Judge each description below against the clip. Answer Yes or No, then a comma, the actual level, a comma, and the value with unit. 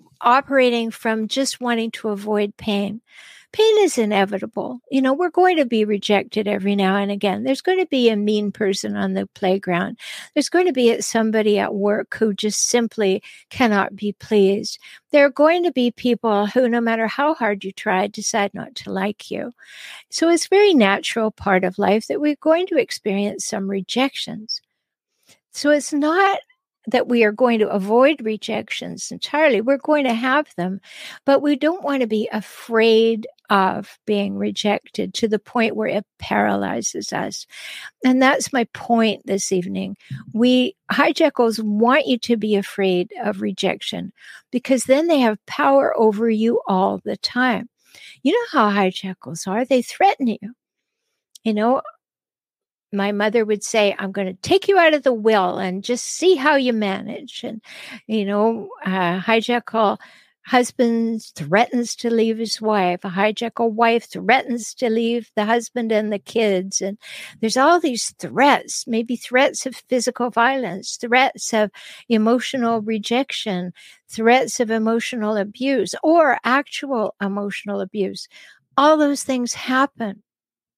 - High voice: Yes, high, 225 Hz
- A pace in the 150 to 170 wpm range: Yes, average, 155 wpm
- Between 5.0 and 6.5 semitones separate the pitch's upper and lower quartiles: No, average, 4.1 semitones